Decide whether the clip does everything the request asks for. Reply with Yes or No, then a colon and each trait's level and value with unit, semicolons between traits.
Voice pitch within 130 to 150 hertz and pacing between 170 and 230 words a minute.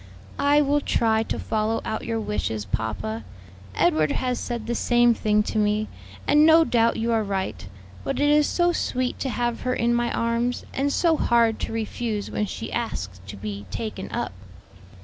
No: high, 230 Hz; average, 185 wpm